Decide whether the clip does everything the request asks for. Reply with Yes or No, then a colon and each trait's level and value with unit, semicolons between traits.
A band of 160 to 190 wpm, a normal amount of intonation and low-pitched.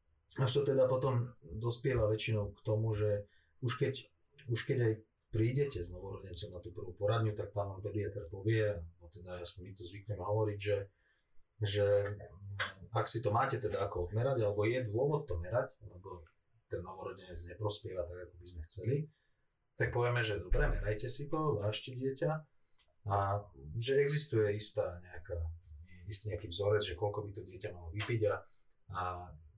Yes: fast, 165 wpm; average, 4.3 semitones; low, 105 Hz